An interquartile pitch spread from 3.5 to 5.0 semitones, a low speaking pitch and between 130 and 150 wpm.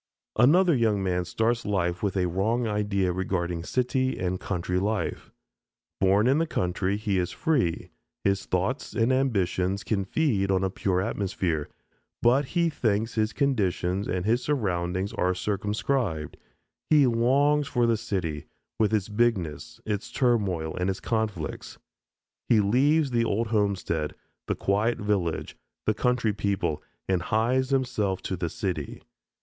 Yes: average, 4.5 semitones; low, 105 Hz; average, 145 wpm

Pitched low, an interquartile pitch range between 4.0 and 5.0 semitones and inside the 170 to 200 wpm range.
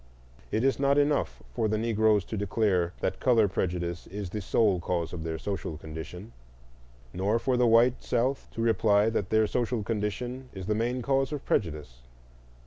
Yes: low, 110 Hz; average, 4.7 semitones; average, 175 wpm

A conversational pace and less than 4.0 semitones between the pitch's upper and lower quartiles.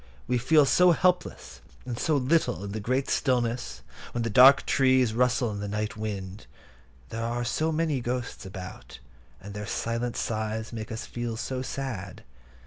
Yes: average, 165 wpm; average, 3.3 semitones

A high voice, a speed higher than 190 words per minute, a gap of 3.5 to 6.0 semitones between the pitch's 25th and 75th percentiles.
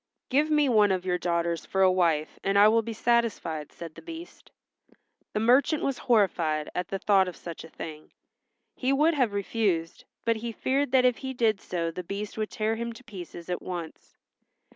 Yes: high, 205 Hz; average, 200 wpm; average, 5.3 semitones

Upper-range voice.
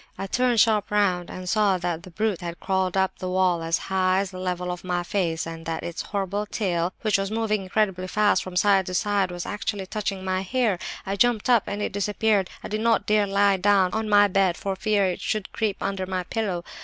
Yes: high, 195 Hz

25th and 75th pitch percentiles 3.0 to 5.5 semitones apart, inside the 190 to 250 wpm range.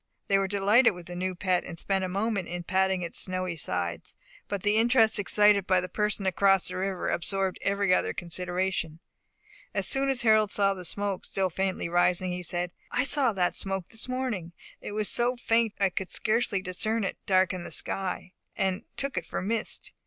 No: narrow, 2.6 semitones; average, 195 wpm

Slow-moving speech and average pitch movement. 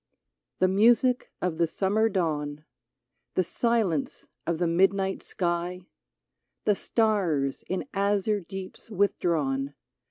Yes: slow, 105 wpm; average, 3.6 semitones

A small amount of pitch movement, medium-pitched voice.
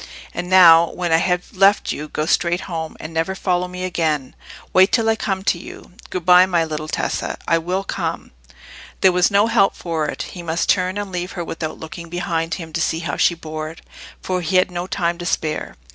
Yes: narrow, 2.2 semitones; medium, 175 Hz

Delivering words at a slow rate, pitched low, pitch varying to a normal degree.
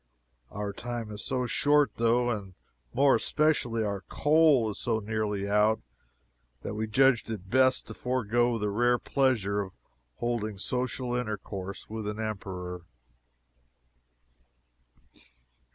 Yes: slow, 120 wpm; low, 110 Hz; average, 3.2 semitones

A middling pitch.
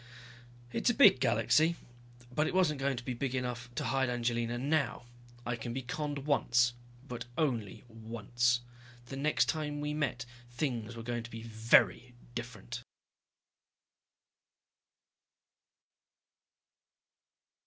No: low, 120 Hz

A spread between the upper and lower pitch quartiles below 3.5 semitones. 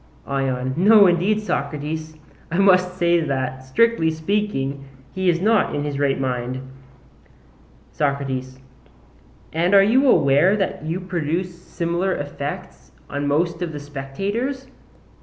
No: average, 5.2 semitones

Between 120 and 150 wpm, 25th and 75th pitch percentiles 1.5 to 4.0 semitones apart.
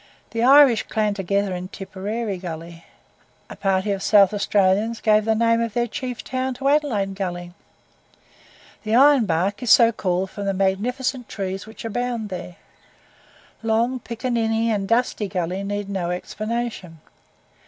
Yes: average, 145 wpm; average, 3.4 semitones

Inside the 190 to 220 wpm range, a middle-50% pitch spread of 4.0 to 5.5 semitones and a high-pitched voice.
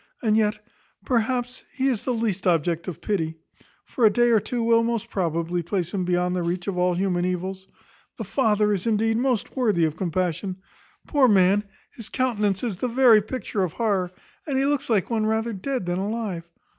Yes: average, 195 wpm; average, 4.5 semitones; high, 205 Hz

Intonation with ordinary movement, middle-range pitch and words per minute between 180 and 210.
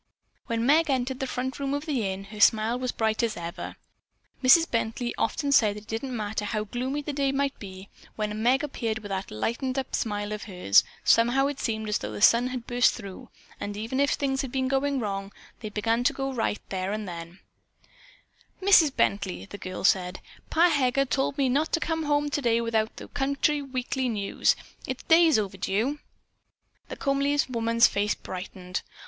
No: average, 4.7 semitones; high, 235 Hz; average, 190 wpm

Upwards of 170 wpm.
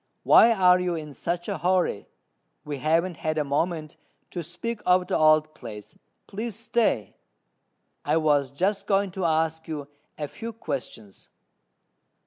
No: average, 145 wpm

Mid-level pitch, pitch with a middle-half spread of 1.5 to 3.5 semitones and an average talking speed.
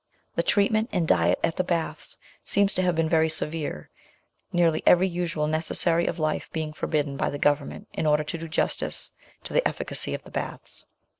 Yes: medium, 160 Hz; narrow, 2.5 semitones; average, 190 wpm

